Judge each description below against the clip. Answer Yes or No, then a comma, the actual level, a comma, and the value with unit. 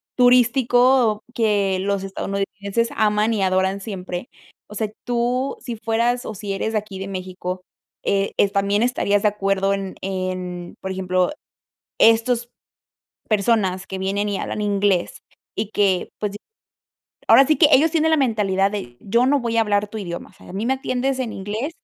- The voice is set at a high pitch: Yes, high, 205 Hz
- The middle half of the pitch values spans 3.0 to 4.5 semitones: Yes, average, 3.4 semitones